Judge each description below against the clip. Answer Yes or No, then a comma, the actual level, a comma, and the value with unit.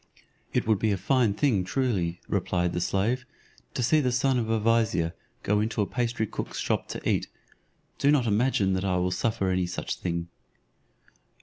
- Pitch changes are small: No, average, 4.8 semitones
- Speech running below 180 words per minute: No, average, 185 wpm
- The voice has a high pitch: No, low, 105 Hz